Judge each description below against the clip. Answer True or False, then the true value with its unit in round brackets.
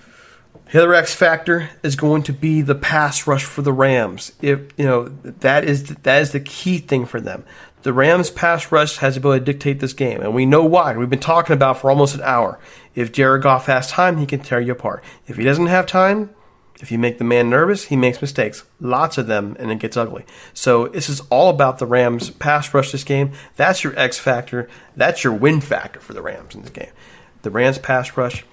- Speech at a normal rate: False (230 wpm)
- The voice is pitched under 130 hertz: False (140 Hz)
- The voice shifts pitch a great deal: False (3.4 semitones)